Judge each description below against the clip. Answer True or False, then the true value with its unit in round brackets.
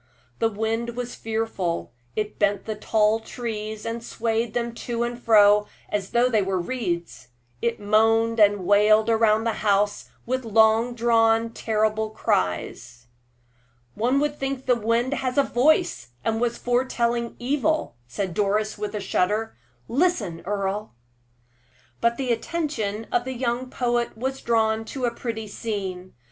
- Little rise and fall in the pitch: True (2.3 semitones)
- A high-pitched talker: True (225 Hz)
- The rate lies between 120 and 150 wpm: True (145 wpm)